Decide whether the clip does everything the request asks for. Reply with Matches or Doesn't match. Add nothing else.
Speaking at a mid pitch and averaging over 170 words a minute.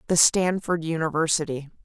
Doesn't match